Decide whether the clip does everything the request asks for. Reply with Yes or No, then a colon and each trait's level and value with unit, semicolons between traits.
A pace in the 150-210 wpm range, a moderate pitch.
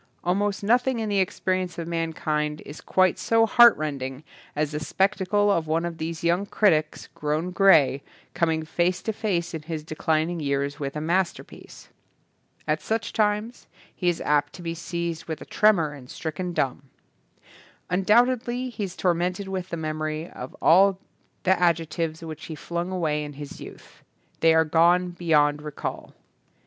Yes: average, 170 wpm; medium, 170 Hz